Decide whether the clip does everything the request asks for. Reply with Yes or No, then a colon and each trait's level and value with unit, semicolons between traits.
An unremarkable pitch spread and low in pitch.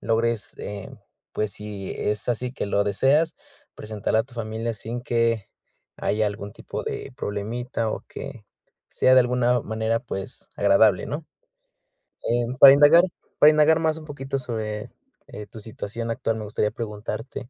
Yes: average, 3.0 semitones; low, 115 Hz